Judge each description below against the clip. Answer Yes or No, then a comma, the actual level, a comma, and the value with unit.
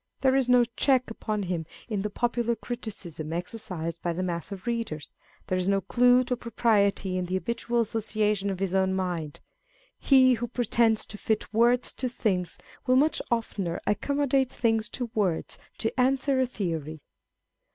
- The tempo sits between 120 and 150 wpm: No, average, 170 wpm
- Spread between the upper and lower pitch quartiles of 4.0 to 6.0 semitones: Yes, average, 4.8 semitones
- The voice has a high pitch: Yes, high, 220 Hz